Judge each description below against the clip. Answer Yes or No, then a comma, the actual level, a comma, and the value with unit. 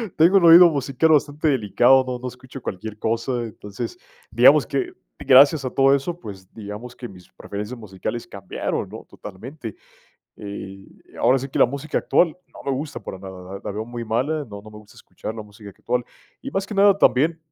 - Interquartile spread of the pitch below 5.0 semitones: No, wide, 5.5 semitones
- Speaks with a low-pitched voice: Yes, low, 125 Hz